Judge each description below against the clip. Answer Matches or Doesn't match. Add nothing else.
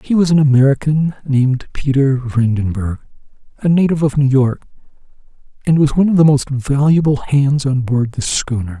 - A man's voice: Matches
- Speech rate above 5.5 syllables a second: Doesn't match